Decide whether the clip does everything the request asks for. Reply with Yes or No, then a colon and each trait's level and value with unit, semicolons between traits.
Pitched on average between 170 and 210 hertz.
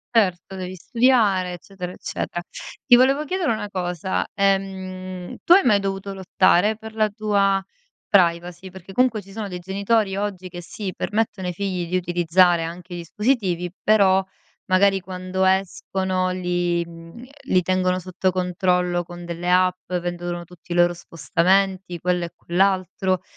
Yes: medium, 185 Hz